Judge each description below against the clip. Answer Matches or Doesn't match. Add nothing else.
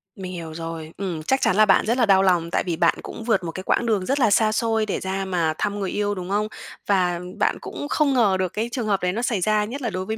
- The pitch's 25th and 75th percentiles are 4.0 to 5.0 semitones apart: Doesn't match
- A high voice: Matches